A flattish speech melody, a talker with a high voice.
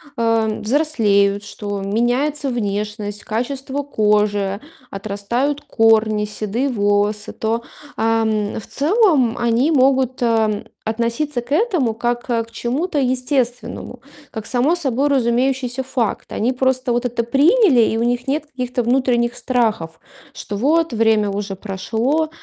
No: average, 3.7 semitones; high, 235 Hz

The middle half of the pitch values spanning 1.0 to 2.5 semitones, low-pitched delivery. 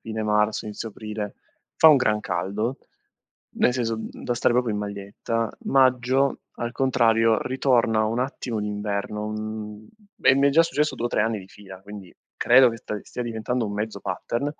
No: average, 2.9 semitones; low, 110 Hz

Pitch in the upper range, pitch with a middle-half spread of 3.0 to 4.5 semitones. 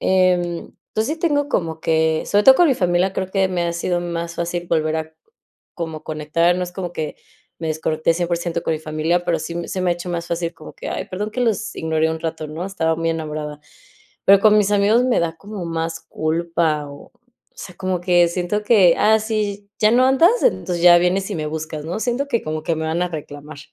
No: medium, 175 Hz; average, 3.4 semitones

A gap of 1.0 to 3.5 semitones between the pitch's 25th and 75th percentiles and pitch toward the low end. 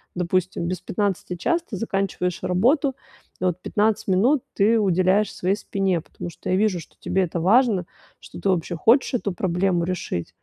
No: average, 2.9 semitones; high, 190 Hz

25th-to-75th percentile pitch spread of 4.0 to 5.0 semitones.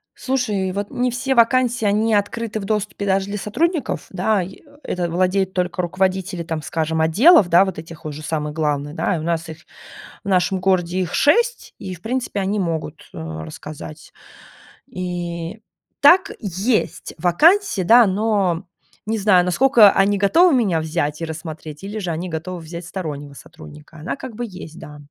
Yes: average, 4.6 semitones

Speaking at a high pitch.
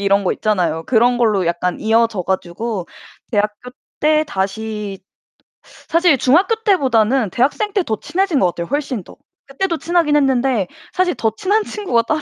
Yes: high, 240 Hz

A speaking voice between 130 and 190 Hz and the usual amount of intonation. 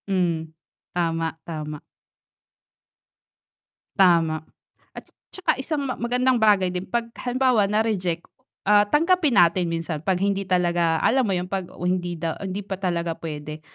Yes: medium, 185 Hz; average, 4.4 semitones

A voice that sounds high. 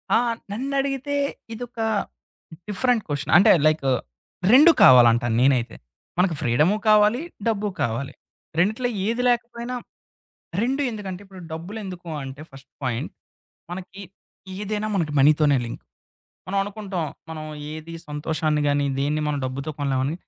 No: medium, 175 Hz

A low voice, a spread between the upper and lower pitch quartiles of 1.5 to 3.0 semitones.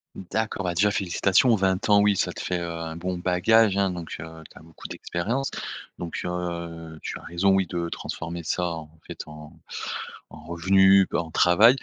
Yes: very low, 90 Hz; narrow, 2.5 semitones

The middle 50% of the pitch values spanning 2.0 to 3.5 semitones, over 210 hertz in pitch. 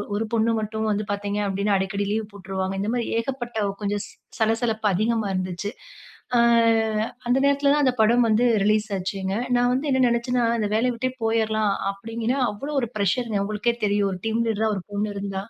Yes: average, 2.8 semitones; high, 220 Hz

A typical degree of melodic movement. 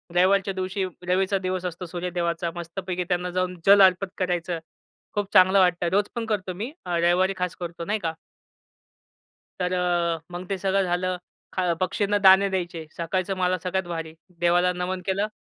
No: narrow, 1.5 semitones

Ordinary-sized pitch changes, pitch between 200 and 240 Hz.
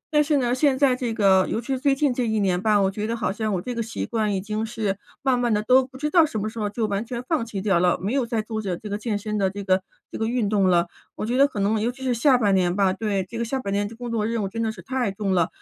Yes: average, 3.6 semitones; high, 220 Hz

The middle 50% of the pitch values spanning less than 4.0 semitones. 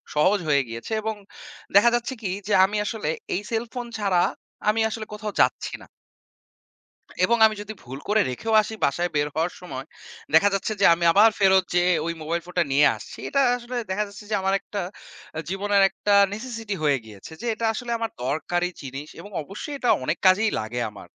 No: average, 5.3 semitones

